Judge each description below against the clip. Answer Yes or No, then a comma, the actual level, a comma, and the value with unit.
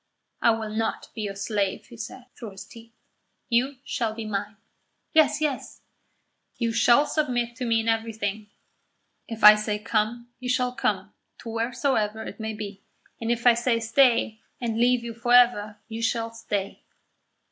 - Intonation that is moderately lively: No, narrow, 2.0 semitones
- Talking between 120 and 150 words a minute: No, average, 170 wpm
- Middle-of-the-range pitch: No, high, 230 Hz